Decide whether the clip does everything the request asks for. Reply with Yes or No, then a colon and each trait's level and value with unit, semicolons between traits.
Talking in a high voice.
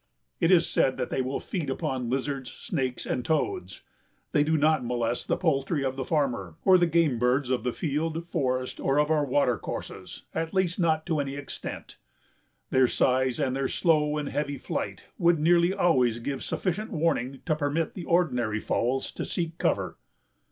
No: medium, 145 Hz